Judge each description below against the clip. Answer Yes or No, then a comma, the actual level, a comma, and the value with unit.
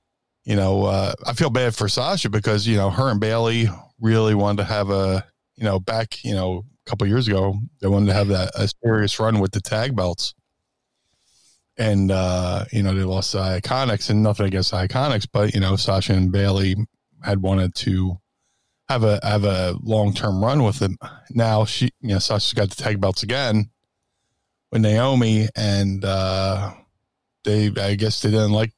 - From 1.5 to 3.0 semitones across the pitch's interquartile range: Yes, average, 2.7 semitones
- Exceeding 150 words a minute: Yes, average, 190 wpm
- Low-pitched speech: Yes, low, 105 Hz